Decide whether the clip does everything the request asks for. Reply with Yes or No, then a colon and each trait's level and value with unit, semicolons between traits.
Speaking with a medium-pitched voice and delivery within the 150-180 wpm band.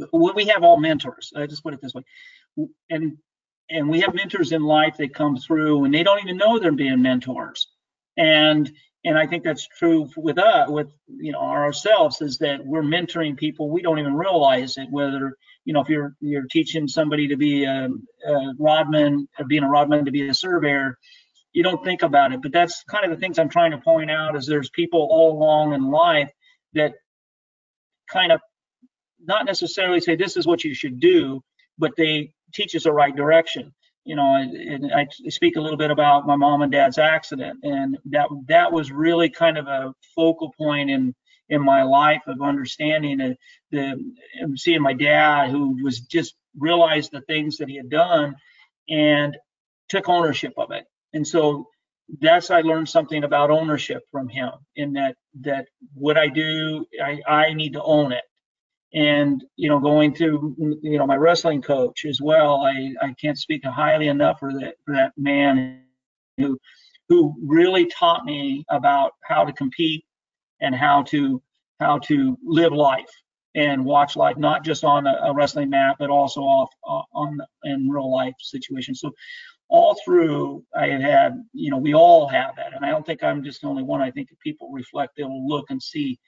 No: medium, 155 Hz; average, 190 wpm